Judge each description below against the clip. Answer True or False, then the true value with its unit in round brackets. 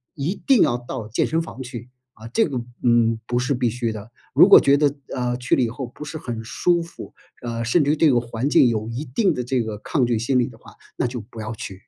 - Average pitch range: True (3.3 semitones)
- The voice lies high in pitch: False (125 Hz)